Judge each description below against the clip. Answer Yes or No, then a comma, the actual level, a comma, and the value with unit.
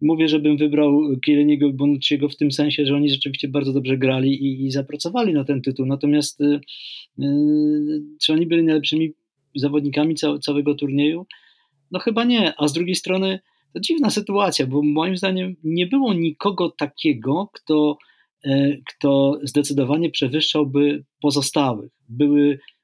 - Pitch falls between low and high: Yes, medium, 150 Hz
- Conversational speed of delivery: Yes, average, 145 wpm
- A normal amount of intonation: No, narrow, 2.1 semitones